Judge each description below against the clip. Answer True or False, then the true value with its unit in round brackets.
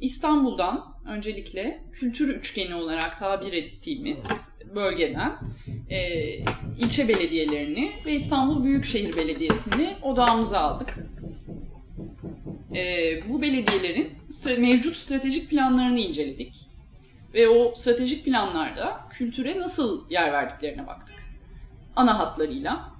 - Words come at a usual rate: False (85 wpm)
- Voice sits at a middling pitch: False (225 Hz)